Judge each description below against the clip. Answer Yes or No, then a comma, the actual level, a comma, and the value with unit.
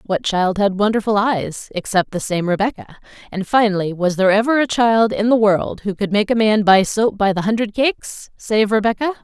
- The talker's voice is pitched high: Yes, high, 210 Hz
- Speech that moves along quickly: Yes, fast, 210 wpm